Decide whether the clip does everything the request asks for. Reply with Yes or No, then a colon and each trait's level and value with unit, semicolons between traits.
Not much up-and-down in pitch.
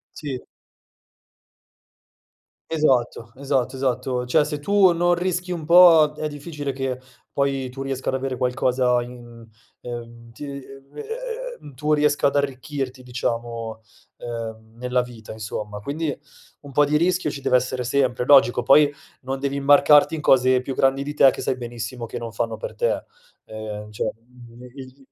No: average, 3.2 semitones